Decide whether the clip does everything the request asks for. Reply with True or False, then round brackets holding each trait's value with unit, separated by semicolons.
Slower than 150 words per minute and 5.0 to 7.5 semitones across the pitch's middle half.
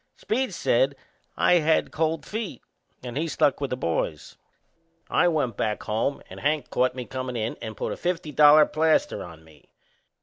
False (175 wpm; 5.4 semitones)